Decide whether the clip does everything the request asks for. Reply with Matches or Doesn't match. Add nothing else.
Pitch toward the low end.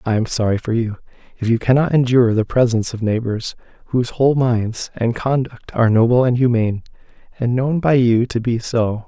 Matches